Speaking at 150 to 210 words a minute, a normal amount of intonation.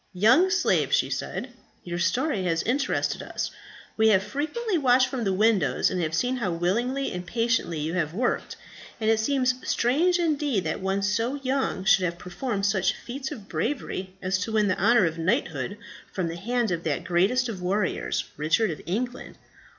No: average, 180 wpm; wide, 5.8 semitones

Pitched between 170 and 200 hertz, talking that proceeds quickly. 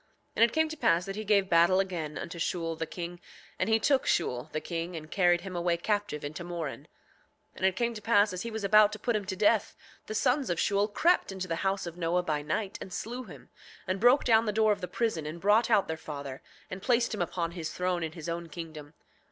Yes: medium, 185 Hz; fast, 250 wpm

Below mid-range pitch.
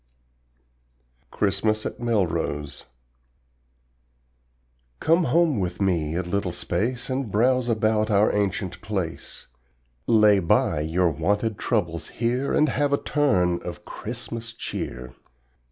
Yes: low, 105 Hz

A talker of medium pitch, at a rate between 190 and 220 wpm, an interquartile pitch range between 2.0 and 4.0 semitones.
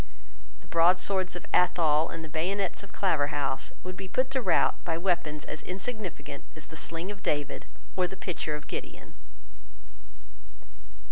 No: medium, 175 Hz; average, 150 wpm; average, 3.3 semitones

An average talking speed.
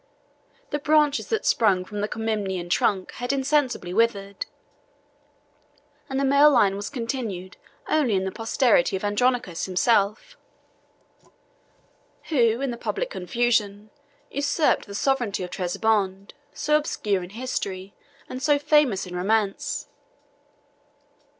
No: slow, 120 wpm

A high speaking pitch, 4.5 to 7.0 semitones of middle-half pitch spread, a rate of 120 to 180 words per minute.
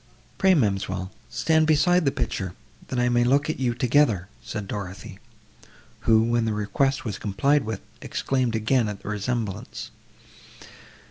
No: low, 115 Hz; average, 4.8 semitones; average, 145 wpm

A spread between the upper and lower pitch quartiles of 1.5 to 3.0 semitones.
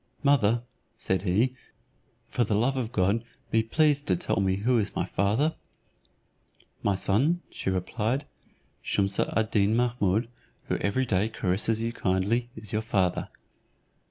No: average, 3.8 semitones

